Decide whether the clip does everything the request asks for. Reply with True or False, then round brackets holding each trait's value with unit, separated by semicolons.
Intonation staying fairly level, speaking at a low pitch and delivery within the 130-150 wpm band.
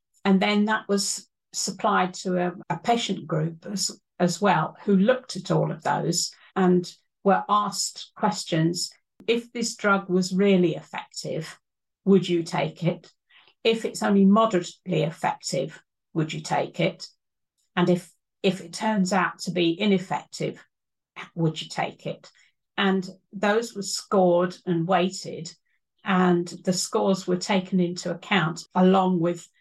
False (2.3 semitones; 185 Hz; 140 wpm)